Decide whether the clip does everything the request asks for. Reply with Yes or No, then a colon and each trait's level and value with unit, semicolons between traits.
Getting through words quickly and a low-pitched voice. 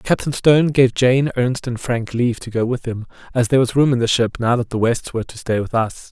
Yes: fast, 275 wpm; low, 120 Hz